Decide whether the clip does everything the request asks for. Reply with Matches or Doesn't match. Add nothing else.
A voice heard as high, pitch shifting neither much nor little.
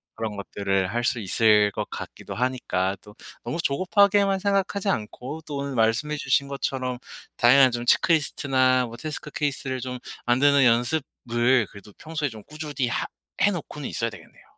Doesn't match